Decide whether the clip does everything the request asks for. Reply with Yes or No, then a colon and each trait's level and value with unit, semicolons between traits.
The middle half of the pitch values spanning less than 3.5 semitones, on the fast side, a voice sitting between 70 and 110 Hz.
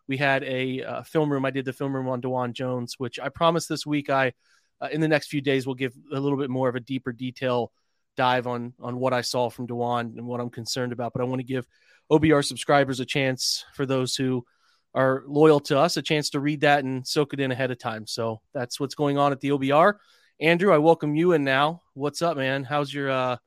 No: narrow, 2.4 semitones; fast, 250 wpm; low, 135 Hz